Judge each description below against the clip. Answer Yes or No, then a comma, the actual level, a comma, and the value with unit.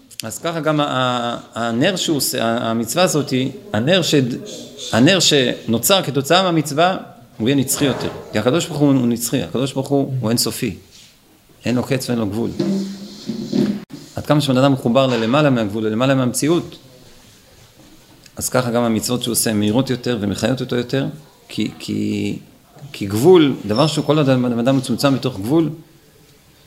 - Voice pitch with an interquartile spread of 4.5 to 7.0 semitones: No, average, 4.1 semitones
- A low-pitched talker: Yes, low, 130 Hz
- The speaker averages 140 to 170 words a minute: Yes, average, 145 wpm